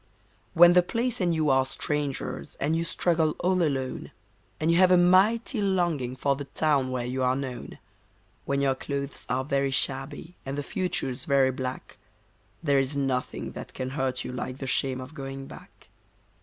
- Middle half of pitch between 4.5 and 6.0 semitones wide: No, average, 4.1 semitones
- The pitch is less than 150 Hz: Yes, medium, 140 Hz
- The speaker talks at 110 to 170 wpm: No, average, 180 wpm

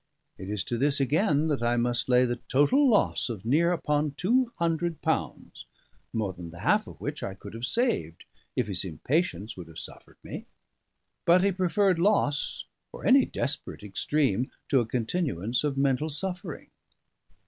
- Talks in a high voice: No, medium, 140 Hz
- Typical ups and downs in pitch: No, wide, 7.2 semitones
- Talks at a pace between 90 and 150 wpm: No, average, 170 wpm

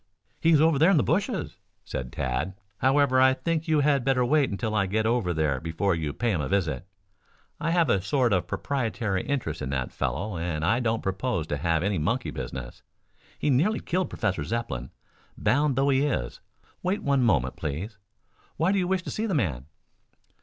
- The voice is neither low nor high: No, low, 110 Hz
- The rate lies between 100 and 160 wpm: No, average, 195 wpm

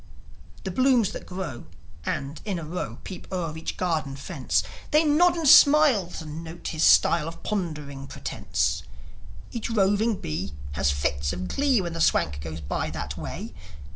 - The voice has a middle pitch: Yes, medium, 165 Hz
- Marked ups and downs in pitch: Yes, wide, 7.5 semitones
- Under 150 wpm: No, average, 165 wpm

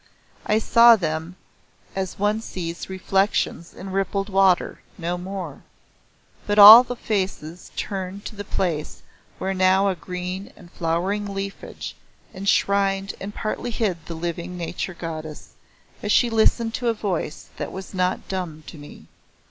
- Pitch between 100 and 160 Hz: No, high, 190 Hz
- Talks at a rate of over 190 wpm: No, average, 140 wpm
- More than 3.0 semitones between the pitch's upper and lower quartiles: No, average, 2.7 semitones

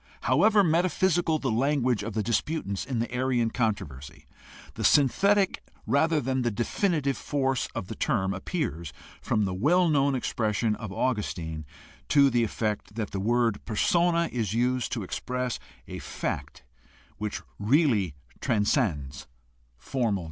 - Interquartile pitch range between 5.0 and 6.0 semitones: Yes, wide, 5.5 semitones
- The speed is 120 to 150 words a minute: Yes, average, 140 wpm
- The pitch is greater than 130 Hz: No, low, 120 Hz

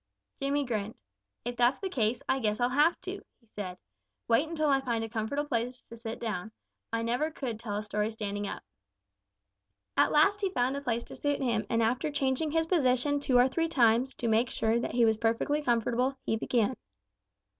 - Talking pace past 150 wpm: Yes, average, 200 wpm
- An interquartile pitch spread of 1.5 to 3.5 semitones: No, average, 3.9 semitones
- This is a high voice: Yes, high, 245 Hz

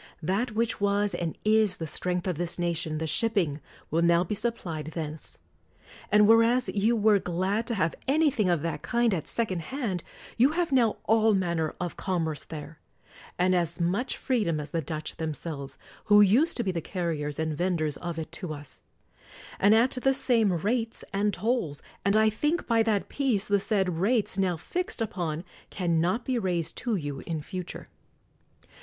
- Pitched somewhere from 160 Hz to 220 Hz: Yes, high, 190 Hz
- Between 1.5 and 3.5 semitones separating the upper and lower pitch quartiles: No, average, 5.3 semitones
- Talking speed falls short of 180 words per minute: No, average, 185 wpm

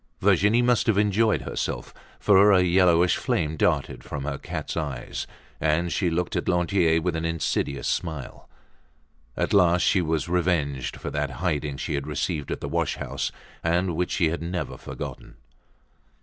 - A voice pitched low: Yes, very low, 85 Hz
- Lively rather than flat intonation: No, average, 3.0 semitones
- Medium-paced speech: Yes, average, 165 wpm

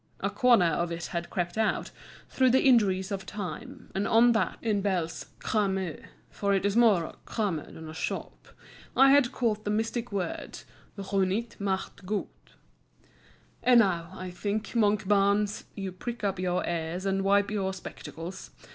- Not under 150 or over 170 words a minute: Yes, average, 160 wpm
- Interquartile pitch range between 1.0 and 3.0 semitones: Yes, average, 2.7 semitones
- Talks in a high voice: Yes, high, 200 Hz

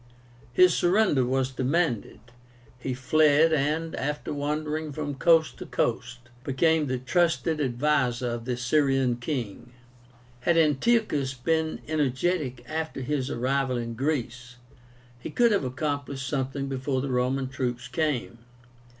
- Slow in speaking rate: Yes, slow, 125 wpm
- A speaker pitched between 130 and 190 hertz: Yes, low, 135 Hz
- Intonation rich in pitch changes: No, average, 3.6 semitones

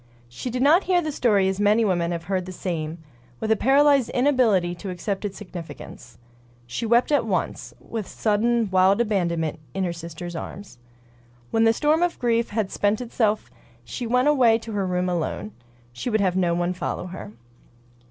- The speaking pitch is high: Yes, high, 205 Hz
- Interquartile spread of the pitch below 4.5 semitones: No, average, 5.0 semitones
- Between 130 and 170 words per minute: No, average, 180 wpm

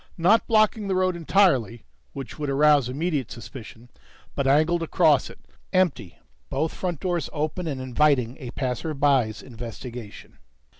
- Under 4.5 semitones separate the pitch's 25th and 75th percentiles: No, wide, 5.4 semitones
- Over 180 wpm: No, average, 145 wpm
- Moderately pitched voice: Yes, medium, 145 Hz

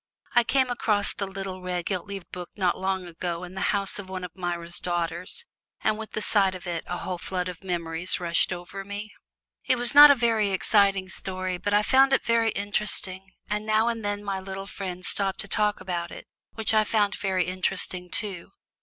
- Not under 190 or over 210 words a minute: Yes, fast, 205 wpm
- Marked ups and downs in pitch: No, narrow, 2.6 semitones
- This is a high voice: Yes, high, 195 Hz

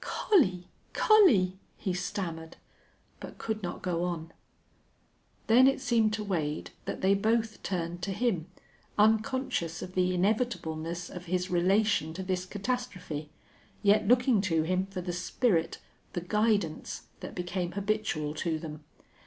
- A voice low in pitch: No, medium, 185 Hz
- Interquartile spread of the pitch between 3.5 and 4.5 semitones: Yes, average, 3.9 semitones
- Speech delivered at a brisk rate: No, average, 140 wpm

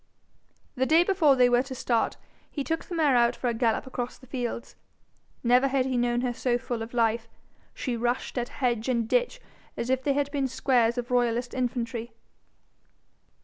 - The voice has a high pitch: Yes, high, 245 Hz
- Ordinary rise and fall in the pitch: No, narrow, 1.9 semitones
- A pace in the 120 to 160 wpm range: No, average, 190 wpm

